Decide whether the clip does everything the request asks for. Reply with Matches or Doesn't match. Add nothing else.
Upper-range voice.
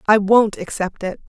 Matches